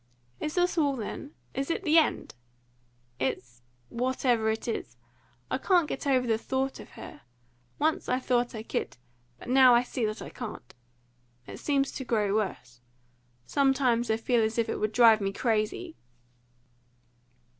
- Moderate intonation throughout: Yes, average, 3.7 semitones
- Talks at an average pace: Yes, average, 160 wpm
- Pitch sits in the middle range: No, high, 245 Hz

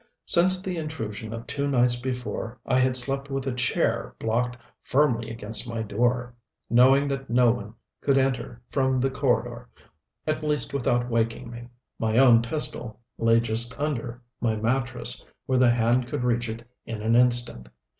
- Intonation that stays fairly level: Yes, narrow, 2.3 semitones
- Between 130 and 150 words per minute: No, average, 165 wpm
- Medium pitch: No, low, 120 Hz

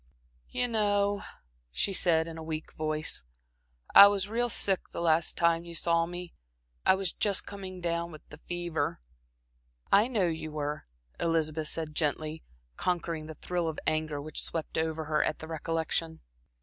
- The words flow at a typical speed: Yes, average, 160 wpm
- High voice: No, medium, 165 Hz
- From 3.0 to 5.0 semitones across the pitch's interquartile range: No, narrow, 2.6 semitones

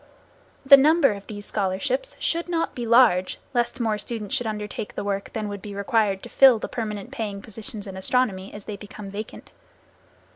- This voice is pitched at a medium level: No, high, 215 Hz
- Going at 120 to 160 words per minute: No, average, 185 wpm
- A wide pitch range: No, average, 3.6 semitones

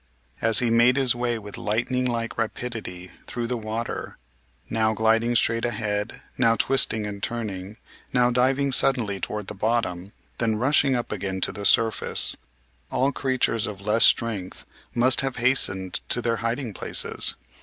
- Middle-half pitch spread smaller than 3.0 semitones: Yes, narrow, 2.6 semitones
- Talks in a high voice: No, low, 115 Hz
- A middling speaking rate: Yes, average, 155 wpm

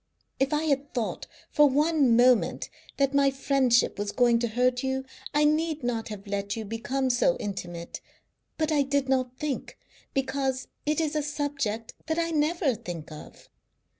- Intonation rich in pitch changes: No, average, 4.1 semitones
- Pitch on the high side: Yes, very high, 265 Hz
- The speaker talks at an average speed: Yes, average, 165 wpm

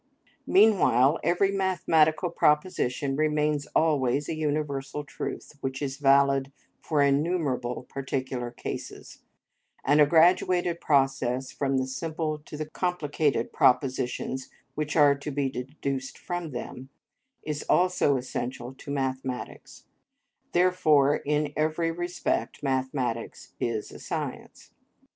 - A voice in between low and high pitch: Yes, medium, 145 Hz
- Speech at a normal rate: No, slow, 110 wpm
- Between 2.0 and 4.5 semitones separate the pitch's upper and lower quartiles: Yes, average, 3.0 semitones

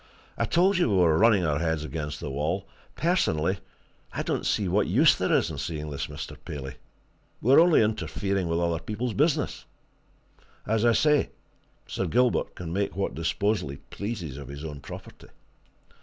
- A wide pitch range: Yes, wide, 6.7 semitones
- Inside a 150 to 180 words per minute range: Yes, average, 170 wpm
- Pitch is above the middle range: No, very low, 95 Hz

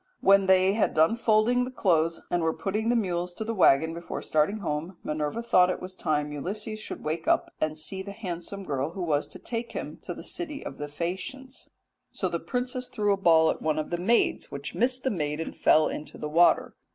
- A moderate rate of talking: No, fast, 225 wpm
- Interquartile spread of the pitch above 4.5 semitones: Yes, wide, 5.6 semitones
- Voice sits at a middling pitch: Yes, medium, 180 Hz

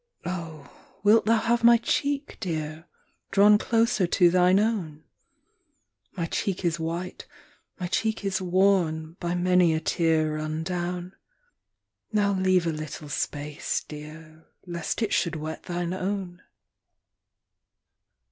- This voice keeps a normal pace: No, slow, 130 wpm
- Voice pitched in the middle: Yes, medium, 175 Hz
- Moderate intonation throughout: Yes, average, 3.7 semitones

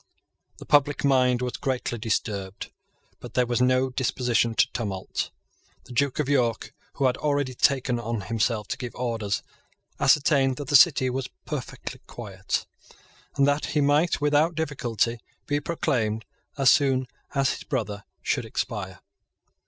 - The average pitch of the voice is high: No, low, 130 Hz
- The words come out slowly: No, average, 145 wpm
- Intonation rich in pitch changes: No, average, 3.3 semitones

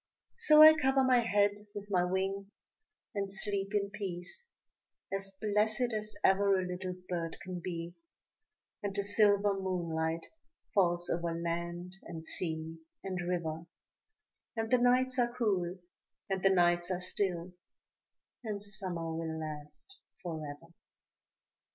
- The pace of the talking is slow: Yes, slow, 130 wpm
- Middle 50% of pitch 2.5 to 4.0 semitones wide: Yes, average, 3.1 semitones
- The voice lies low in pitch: No, high, 190 Hz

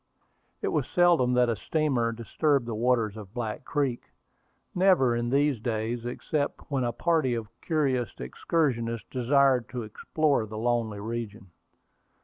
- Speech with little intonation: No, average, 3.7 semitones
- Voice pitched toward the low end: Yes, low, 120 Hz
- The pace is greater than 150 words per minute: No, average, 140 wpm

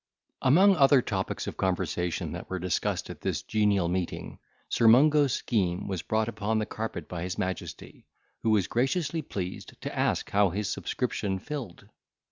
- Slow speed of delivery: No, average, 160 wpm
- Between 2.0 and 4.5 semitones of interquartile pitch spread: No, wide, 5.6 semitones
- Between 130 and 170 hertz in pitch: No, low, 105 Hz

